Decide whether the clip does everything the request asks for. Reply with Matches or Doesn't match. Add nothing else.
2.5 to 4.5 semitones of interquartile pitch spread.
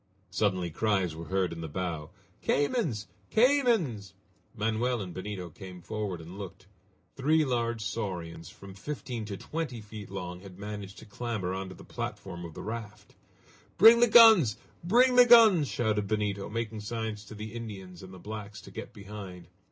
Matches